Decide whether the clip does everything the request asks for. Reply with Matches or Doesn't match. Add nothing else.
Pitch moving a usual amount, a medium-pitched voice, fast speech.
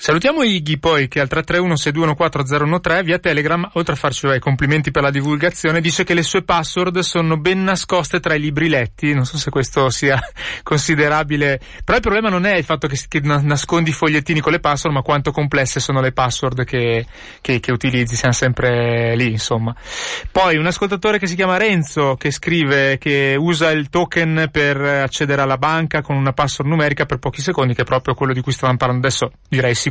Matches